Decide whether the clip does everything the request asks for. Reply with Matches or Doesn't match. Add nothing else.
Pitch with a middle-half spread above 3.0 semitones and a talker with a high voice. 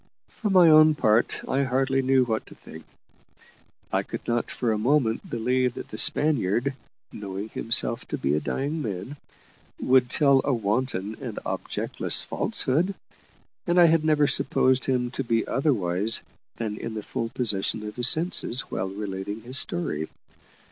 Doesn't match